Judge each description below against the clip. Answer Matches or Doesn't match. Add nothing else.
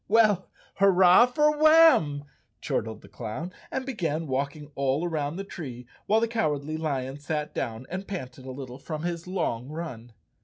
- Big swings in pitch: Matches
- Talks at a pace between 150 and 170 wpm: Matches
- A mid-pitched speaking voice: Matches